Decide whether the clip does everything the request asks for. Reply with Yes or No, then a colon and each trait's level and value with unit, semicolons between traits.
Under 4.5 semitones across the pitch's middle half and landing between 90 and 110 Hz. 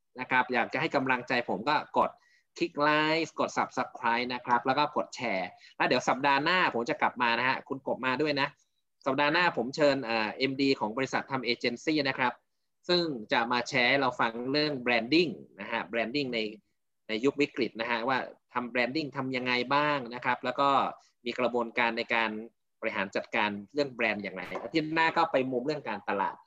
No: average, 3.3 semitones; low, 125 Hz